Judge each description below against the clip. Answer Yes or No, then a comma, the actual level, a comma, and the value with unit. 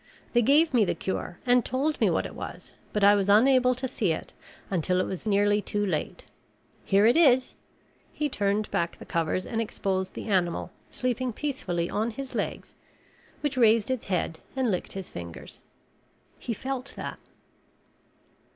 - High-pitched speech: Yes, high, 215 Hz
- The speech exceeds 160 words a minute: Yes, average, 170 wpm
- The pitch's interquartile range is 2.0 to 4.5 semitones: No, average, 5.2 semitones